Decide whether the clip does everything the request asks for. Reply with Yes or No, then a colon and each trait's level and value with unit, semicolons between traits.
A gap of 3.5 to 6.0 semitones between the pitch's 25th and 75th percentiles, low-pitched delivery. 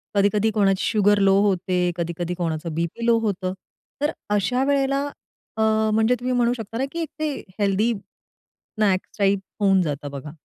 No: average, 4.3 semitones; high, 200 Hz